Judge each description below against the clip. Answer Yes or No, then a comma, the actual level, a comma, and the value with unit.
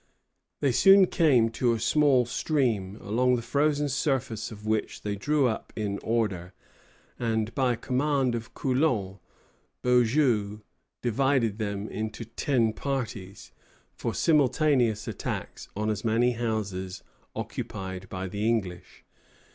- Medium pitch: No, low, 115 Hz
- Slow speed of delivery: Yes, slow, 125 wpm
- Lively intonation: No, average, 3.9 semitones